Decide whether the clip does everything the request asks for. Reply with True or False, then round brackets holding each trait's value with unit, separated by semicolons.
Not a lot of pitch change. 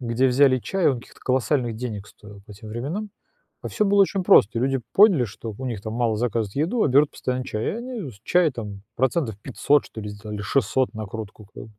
False (5.0 semitones)